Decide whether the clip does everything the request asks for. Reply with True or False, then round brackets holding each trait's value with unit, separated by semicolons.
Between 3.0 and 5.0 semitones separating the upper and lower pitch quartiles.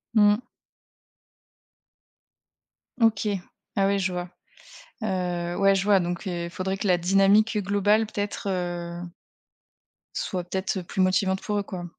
False (2.4 semitones)